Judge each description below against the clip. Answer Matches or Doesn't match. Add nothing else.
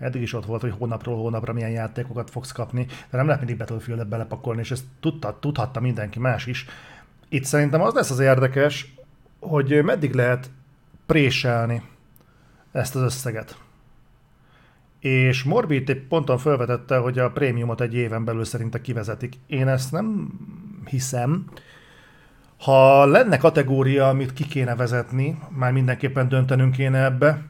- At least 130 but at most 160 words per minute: Matches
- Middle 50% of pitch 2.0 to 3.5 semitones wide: Matches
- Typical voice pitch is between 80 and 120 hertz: Doesn't match